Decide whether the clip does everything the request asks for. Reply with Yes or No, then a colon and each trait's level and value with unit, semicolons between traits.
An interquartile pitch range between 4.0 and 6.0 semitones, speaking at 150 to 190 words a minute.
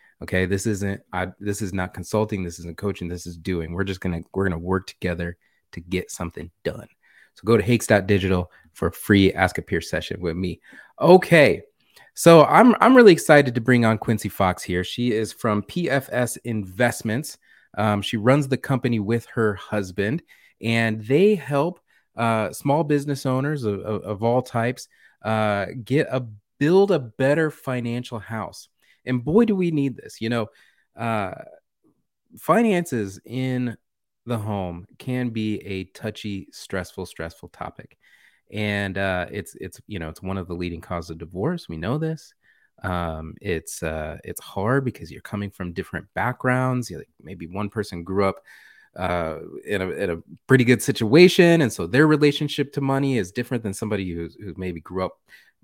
Yes: wide, 5.6 semitones; average, 175 wpm